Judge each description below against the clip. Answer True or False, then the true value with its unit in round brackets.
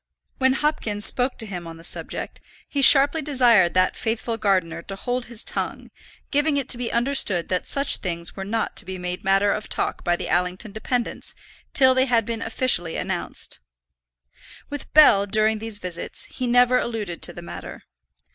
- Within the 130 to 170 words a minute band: False (180 wpm)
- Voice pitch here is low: False (220 Hz)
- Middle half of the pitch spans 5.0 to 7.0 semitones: True (5.5 semitones)